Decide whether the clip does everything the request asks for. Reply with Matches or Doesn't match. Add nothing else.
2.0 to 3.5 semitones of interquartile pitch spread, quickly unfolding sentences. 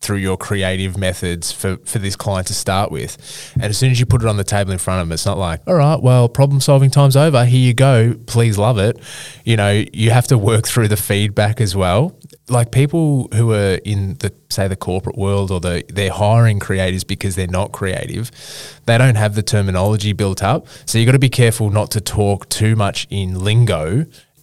Doesn't match